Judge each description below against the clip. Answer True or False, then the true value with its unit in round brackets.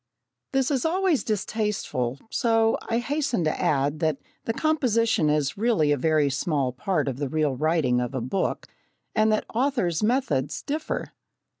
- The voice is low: False (180 Hz)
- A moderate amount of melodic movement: False (8.5 semitones)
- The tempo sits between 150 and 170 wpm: True (155 wpm)